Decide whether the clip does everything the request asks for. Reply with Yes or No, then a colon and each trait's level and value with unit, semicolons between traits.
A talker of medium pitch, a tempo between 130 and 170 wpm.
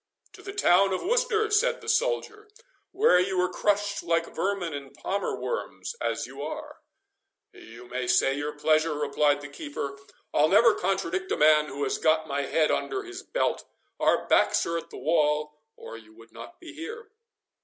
No: medium, 170 Hz; average, 180 wpm